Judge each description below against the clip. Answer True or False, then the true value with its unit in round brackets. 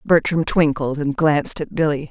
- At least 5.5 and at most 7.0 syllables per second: False (5.0 syllables/s)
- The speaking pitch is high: False (150 Hz)